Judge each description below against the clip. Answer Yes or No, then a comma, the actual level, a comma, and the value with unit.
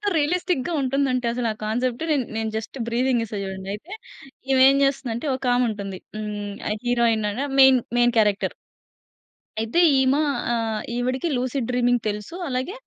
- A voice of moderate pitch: No, high, 245 Hz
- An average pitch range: Yes, average, 3.2 semitones